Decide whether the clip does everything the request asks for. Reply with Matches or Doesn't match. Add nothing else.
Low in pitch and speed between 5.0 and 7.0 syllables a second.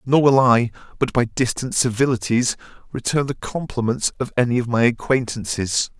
Matches